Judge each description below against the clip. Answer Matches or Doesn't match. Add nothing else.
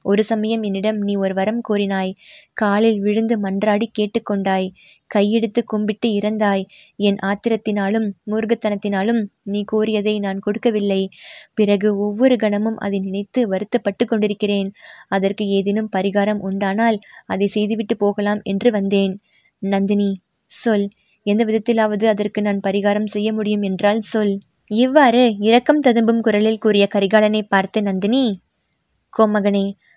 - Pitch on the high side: Matches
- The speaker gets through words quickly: Doesn't match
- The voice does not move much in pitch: Matches